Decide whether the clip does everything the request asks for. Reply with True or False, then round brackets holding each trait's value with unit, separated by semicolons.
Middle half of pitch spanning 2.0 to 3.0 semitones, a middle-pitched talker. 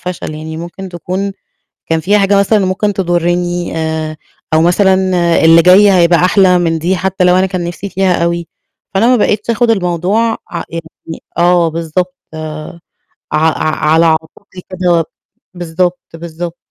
True (2.5 semitones; 175 Hz)